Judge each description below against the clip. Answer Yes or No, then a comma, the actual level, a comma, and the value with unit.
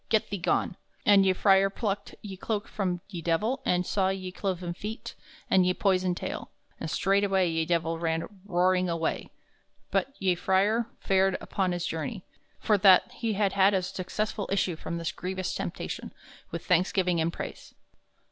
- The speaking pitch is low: No, high, 190 Hz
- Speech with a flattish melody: Yes, narrow, 2.1 semitones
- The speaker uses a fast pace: No, average, 165 wpm